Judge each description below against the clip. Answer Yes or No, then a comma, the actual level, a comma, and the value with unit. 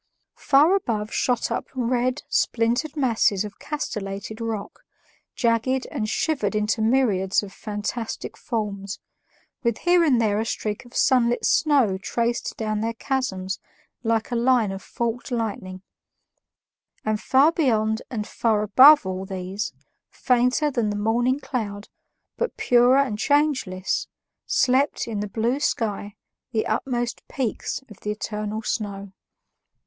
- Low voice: No, high, 230 Hz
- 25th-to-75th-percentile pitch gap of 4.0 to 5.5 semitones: No, average, 3.5 semitones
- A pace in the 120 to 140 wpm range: Yes, slow, 135 wpm